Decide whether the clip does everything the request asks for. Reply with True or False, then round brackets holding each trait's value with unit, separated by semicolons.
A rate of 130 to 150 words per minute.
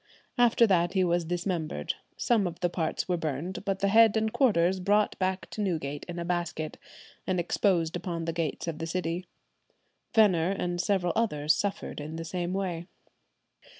False (175 wpm)